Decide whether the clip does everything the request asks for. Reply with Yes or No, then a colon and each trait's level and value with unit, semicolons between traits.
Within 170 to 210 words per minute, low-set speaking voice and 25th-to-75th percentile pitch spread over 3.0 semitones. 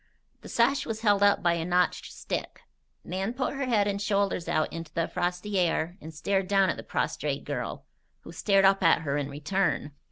No: average, 200 wpm; high, 190 Hz; average, 3.4 semitones